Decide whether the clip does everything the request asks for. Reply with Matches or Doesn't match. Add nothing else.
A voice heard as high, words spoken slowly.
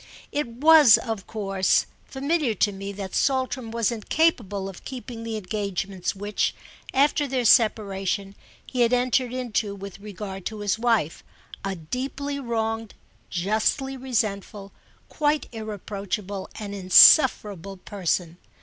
Matches